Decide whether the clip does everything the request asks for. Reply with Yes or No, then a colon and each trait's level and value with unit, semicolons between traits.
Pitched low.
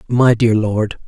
Yes: low, 115 Hz